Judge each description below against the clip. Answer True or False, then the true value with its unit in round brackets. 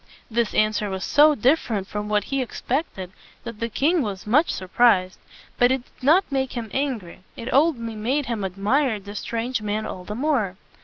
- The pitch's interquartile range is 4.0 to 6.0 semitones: True (4.4 semitones)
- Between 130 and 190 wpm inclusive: False (200 wpm)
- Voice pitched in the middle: False (230 Hz)